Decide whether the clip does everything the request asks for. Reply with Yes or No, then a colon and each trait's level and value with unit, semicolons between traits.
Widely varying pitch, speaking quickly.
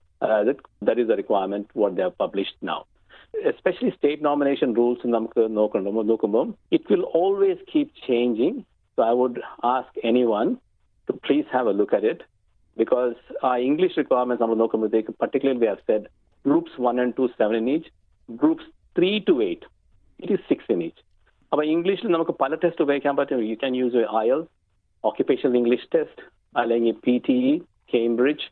Yes: wide, 7.6 semitones; fast, 145 wpm